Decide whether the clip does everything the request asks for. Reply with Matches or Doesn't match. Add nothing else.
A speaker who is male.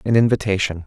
Matches